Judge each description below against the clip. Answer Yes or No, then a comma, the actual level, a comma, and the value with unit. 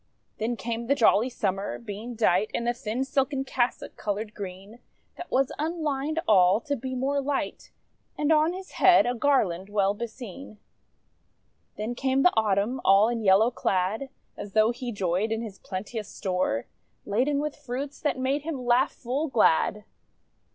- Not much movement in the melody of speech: No, average, 4.8 semitones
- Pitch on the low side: No, high, 235 Hz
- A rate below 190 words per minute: Yes, average, 160 wpm